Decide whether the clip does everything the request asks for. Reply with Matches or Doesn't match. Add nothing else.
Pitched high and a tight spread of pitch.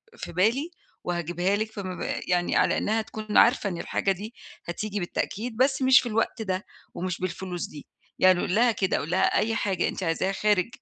Doesn't match